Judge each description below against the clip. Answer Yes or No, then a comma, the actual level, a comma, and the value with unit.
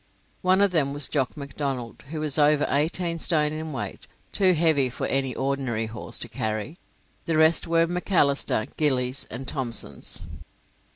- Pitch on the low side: No, medium, 145 Hz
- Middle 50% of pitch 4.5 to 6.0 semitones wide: No, average, 3.6 semitones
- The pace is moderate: Yes, average, 155 wpm